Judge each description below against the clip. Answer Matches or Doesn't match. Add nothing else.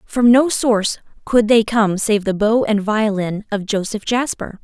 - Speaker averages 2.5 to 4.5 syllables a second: Matches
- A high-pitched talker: Matches